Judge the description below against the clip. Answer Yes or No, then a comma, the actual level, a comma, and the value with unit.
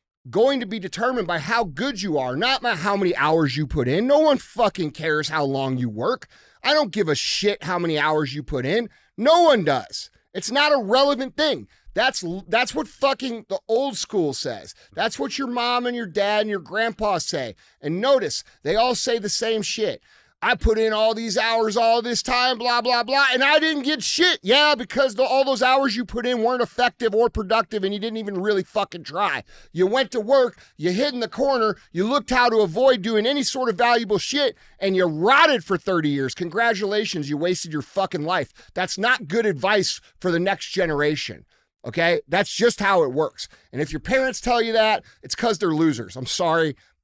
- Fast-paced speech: Yes, fast, 215 wpm